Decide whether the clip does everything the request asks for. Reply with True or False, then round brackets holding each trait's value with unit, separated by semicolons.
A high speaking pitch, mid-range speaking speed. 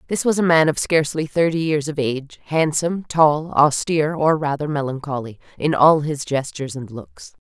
False (150 Hz; 175 wpm)